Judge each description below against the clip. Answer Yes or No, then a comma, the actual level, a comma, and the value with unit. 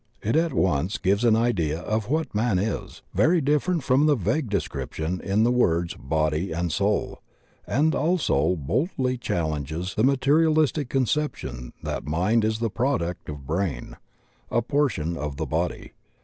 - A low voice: Yes, low, 110 Hz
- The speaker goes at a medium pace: Yes, average, 150 wpm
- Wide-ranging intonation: Yes, wide, 8.7 semitones